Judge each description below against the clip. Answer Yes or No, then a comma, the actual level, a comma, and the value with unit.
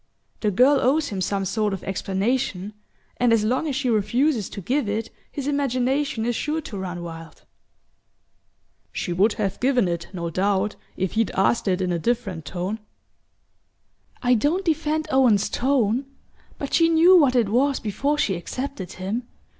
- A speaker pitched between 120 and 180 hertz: No, high, 225 Hz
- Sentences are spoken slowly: No, average, 165 wpm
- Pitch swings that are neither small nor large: No, wide, 6.0 semitones